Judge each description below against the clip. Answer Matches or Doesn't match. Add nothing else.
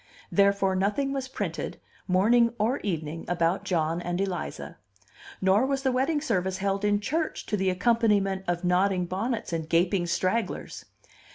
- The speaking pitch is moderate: Doesn't match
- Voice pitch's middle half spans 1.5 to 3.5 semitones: Doesn't match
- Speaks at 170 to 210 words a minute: Doesn't match